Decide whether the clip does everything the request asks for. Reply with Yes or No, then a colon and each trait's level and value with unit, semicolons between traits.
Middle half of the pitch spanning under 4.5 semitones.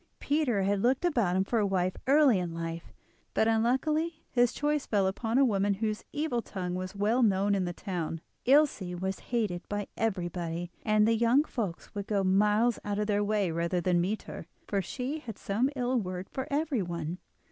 No: average, 4.8 semitones